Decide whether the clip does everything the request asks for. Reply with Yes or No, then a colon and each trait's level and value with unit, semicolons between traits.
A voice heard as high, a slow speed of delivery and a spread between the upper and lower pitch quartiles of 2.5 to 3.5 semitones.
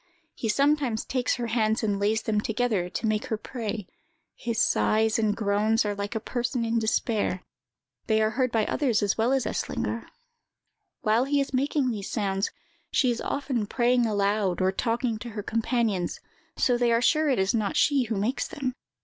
No: high, 225 Hz; average, 185 wpm; average, 2.8 semitones